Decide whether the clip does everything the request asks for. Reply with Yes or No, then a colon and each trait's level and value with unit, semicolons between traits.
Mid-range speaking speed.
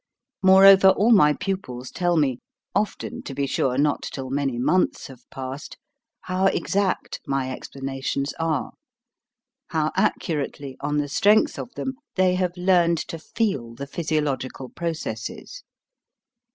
No: slow, 130 wpm